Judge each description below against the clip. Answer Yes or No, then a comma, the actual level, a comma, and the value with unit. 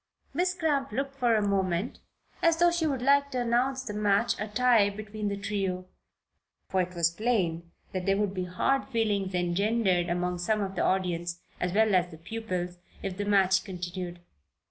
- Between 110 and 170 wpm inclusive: No, average, 180 wpm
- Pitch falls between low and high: No, high, 200 Hz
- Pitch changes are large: No, average, 4.6 semitones